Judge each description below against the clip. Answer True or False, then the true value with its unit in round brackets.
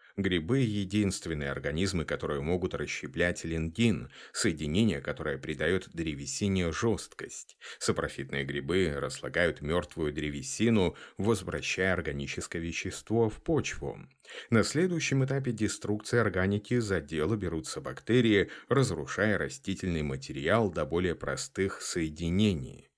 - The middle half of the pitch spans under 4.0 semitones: False (5.4 semitones)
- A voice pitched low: True (95 Hz)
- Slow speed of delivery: True (100 wpm)